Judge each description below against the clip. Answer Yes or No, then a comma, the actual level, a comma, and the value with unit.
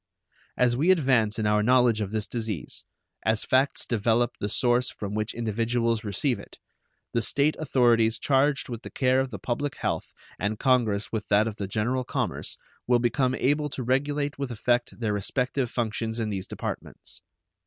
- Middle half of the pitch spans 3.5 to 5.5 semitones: No, average, 3.0 semitones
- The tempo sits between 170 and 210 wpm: Yes, average, 175 wpm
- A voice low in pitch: Yes, low, 120 Hz